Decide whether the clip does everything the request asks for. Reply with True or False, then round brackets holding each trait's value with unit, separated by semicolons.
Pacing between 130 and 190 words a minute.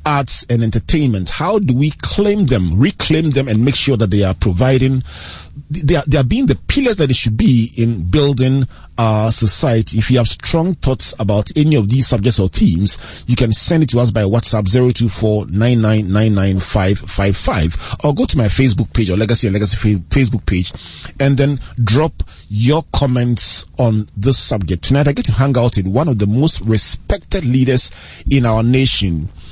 False (205 wpm)